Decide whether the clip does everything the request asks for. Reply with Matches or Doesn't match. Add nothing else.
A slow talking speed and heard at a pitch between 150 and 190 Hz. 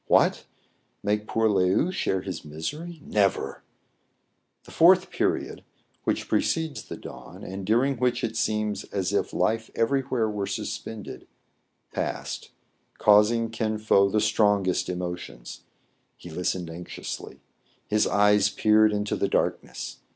Doesn't match